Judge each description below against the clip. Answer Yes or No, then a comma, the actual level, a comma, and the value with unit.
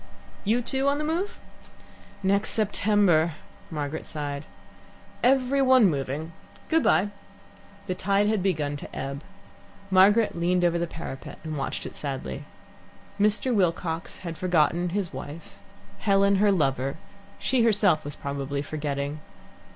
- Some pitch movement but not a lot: No, wide, 5.9 semitones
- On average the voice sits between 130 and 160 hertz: No, medium, 175 Hz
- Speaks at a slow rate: Yes, slow, 130 wpm